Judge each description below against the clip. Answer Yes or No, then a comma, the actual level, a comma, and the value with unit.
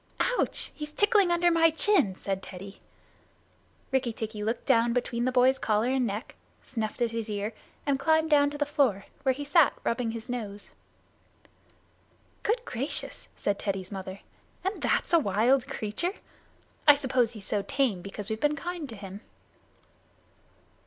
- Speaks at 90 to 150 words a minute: No, average, 160 wpm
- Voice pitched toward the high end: Yes, high, 245 Hz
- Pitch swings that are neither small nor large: No, wide, 5.7 semitones